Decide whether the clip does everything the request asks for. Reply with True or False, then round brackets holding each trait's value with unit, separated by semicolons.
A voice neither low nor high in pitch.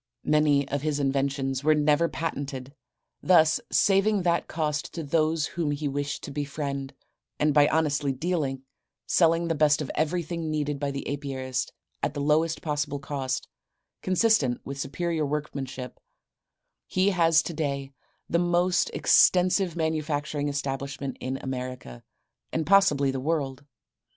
True (150 Hz)